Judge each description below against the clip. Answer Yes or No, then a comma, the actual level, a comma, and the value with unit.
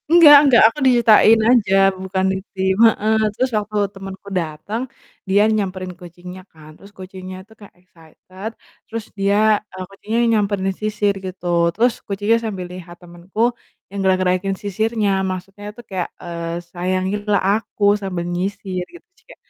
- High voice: Yes, high, 195 Hz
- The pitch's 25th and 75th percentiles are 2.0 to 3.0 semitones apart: Yes, narrow, 2.6 semitones